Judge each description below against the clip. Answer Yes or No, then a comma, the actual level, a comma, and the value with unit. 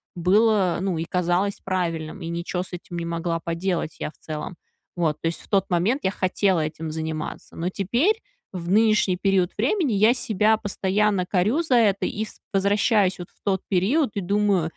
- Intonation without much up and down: No, average, 3.6 semitones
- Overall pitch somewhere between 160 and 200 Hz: Yes, high, 190 Hz